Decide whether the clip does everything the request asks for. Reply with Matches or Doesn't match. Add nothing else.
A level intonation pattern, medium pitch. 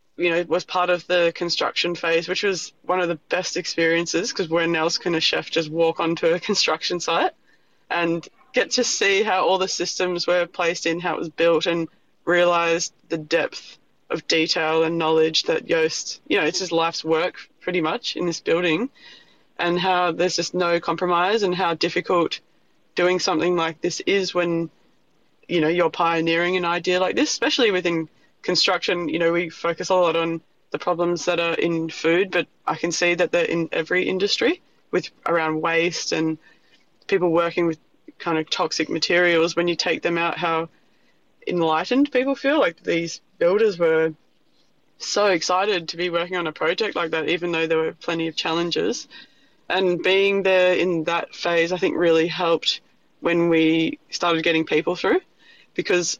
Matches